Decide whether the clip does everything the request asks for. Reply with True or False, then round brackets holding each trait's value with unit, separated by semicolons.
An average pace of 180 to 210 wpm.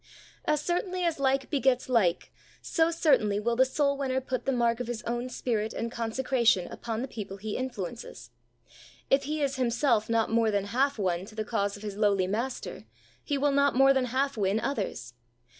True (195 wpm)